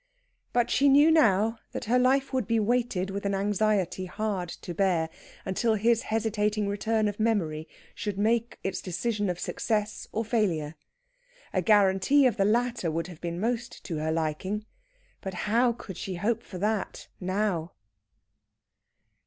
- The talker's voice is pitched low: No, high, 210 Hz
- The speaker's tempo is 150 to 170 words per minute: Yes, average, 155 wpm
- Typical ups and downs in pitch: Yes, average, 3.6 semitones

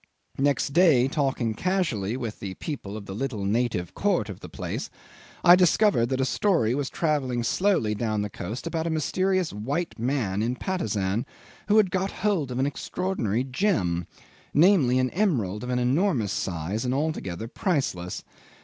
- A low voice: Yes, low, 130 Hz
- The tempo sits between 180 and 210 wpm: No, average, 165 wpm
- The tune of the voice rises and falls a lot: Yes, wide, 8.1 semitones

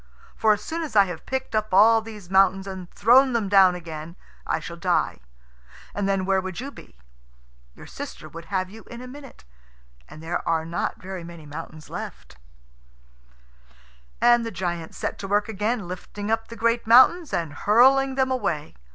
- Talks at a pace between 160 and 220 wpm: Yes, average, 180 wpm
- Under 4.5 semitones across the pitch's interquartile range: No, average, 4.9 semitones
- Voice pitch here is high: Yes, high, 200 Hz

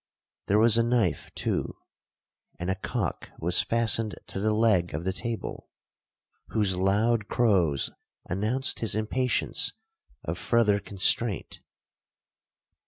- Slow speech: Yes, slow, 115 wpm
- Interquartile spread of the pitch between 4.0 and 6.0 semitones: No, average, 3.5 semitones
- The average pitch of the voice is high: No, low, 105 Hz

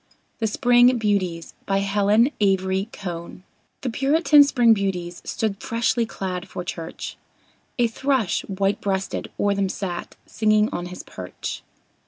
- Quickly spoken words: No, slow, 135 wpm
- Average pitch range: Yes, average, 3.5 semitones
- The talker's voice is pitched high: Yes, high, 200 Hz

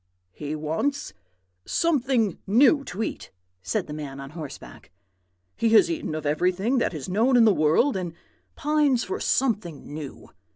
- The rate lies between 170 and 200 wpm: No, average, 155 wpm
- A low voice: No, high, 190 Hz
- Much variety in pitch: Yes, wide, 8.7 semitones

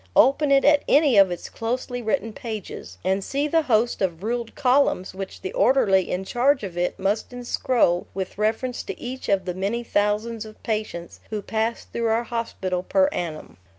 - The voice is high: Yes, high, 225 Hz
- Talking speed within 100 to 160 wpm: No, average, 185 wpm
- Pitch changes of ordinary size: Yes, average, 4.7 semitones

